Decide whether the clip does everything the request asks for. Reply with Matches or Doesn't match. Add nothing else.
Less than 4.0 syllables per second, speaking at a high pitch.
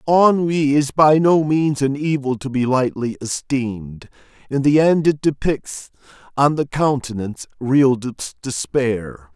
Doesn't match